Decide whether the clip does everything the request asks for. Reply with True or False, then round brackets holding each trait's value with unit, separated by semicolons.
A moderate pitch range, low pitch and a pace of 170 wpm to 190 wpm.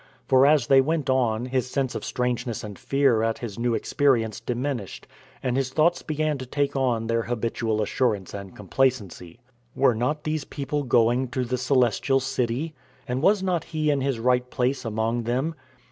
True (3.1 semitones; 125 Hz; 175 wpm)